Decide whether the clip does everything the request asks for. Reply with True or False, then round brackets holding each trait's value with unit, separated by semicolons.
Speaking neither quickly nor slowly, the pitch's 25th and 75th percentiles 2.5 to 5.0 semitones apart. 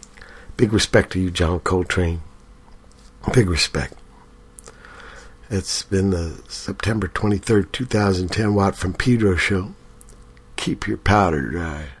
False (110 wpm; 3.9 semitones)